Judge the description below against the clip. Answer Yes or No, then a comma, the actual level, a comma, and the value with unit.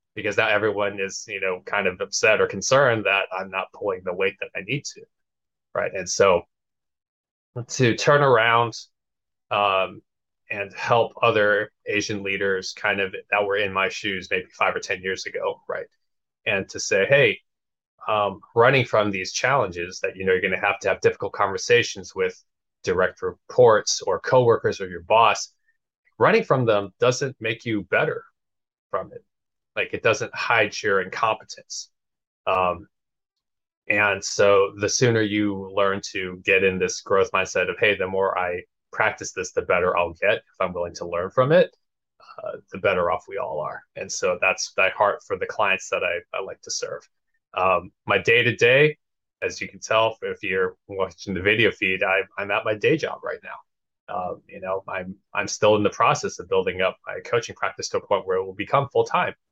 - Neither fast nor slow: Yes, average, 190 wpm